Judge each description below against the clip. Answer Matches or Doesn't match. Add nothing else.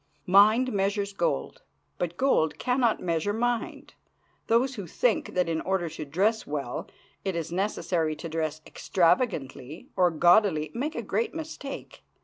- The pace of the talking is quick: Doesn't match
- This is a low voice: Doesn't match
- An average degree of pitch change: Doesn't match